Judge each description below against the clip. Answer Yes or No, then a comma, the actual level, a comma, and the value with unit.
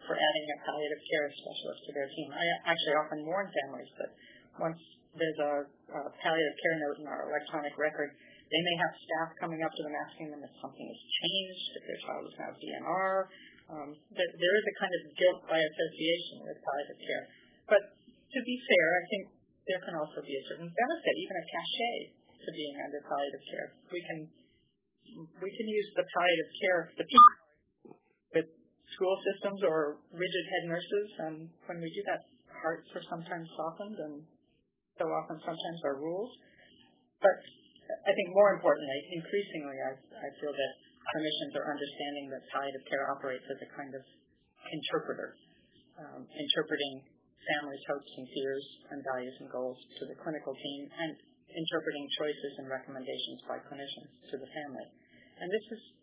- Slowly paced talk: No, average, 170 wpm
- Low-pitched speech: No, medium, 160 Hz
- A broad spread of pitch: No, average, 3.9 semitones